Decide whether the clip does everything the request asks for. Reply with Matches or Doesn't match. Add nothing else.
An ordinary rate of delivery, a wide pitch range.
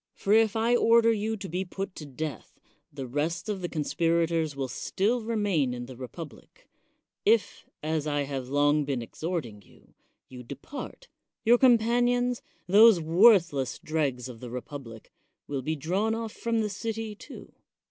Matches